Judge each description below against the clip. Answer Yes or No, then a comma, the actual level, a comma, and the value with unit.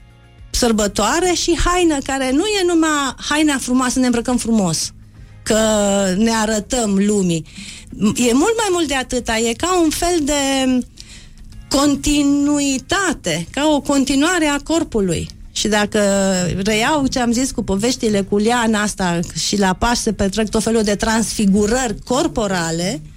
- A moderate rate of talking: Yes, average, 140 wpm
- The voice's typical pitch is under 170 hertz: No, high, 235 Hz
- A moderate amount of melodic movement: No, wide, 5.7 semitones